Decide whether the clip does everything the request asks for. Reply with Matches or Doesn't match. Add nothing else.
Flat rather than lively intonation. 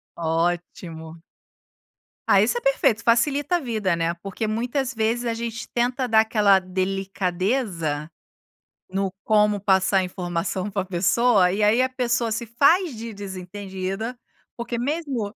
Doesn't match